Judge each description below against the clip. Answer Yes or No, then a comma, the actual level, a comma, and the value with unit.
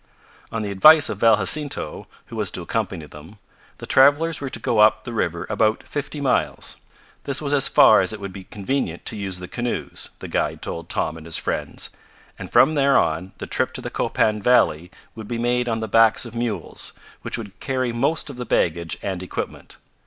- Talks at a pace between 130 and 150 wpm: No, fast, 205 wpm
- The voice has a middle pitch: No, low, 110 Hz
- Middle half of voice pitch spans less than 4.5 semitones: No, average, 5.3 semitones